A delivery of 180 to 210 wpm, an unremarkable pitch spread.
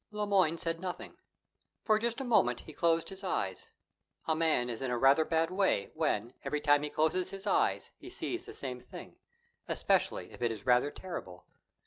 No: average, 195 wpm; wide, 6.9 semitones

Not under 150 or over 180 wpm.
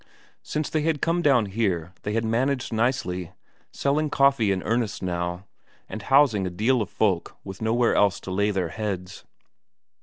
Yes: average, 170 wpm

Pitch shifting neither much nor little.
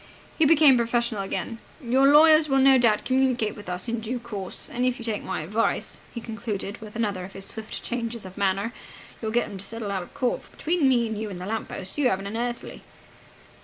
Yes: average, 3.7 semitones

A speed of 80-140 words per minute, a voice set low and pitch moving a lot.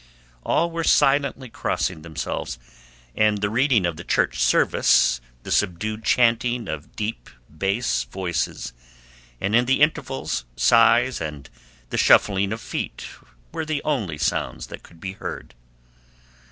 Yes: slow, 135 wpm; low, 105 Hz; wide, 6.7 semitones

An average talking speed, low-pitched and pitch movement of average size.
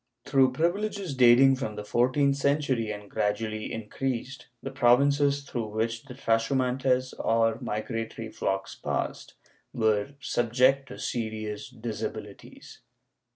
No: slow, 115 wpm; low, 120 Hz; average, 3.6 semitones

